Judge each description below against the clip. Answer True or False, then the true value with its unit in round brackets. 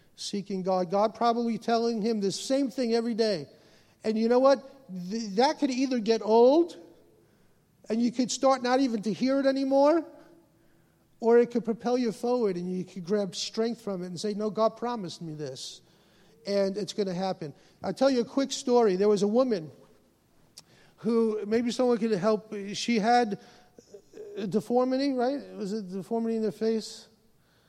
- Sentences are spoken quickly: False (180 wpm)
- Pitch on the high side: True (225 Hz)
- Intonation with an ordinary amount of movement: True (3.4 semitones)